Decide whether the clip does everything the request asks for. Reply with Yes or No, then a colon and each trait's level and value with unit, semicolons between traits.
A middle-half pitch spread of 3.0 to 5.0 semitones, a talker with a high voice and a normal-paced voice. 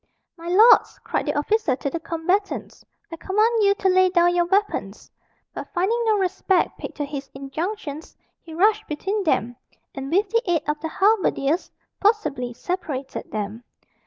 No: wide, 5.4 semitones; very high, 350 Hz; average, 160 wpm